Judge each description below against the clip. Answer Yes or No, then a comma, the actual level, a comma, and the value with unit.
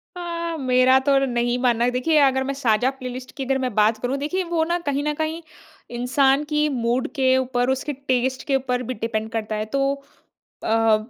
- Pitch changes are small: Yes, narrow, 2.3 semitones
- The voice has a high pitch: Yes, very high, 260 Hz